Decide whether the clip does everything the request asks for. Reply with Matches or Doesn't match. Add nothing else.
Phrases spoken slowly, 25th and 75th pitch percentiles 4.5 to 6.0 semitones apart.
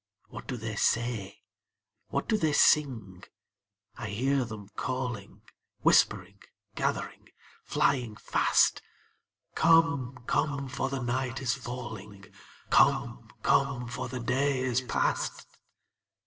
Doesn't match